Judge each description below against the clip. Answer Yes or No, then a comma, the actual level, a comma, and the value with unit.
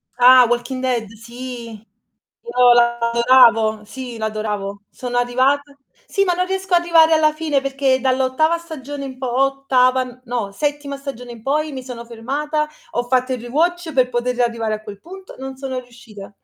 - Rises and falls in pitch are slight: No, average, 3.1 semitones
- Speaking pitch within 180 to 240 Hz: No, very high, 255 Hz